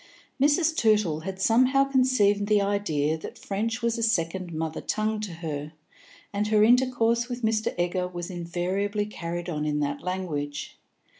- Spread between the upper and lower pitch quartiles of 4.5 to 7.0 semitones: Yes, average, 4.9 semitones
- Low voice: No, high, 200 Hz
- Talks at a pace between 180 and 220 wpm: No, average, 155 wpm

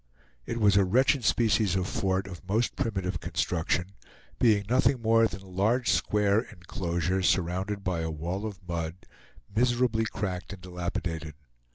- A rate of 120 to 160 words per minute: Yes, average, 150 wpm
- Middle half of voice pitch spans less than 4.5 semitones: Yes, average, 3.7 semitones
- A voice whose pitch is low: Yes, very low, 95 Hz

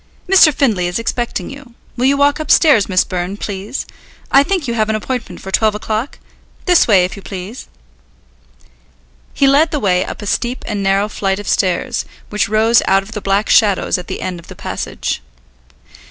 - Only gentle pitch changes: No, average, 5.0 semitones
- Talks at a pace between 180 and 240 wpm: Yes, average, 190 wpm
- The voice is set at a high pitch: Yes, high, 215 Hz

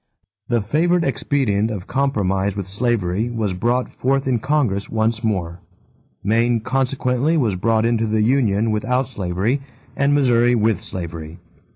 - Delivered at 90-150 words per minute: Yes, average, 140 wpm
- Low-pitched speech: Yes, low, 115 Hz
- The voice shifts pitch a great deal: No, average, 4.2 semitones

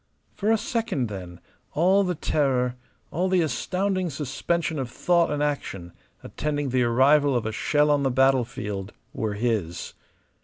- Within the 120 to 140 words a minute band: No, average, 150 wpm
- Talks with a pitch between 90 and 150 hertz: Yes, medium, 140 Hz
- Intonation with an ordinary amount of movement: No, wide, 6.0 semitones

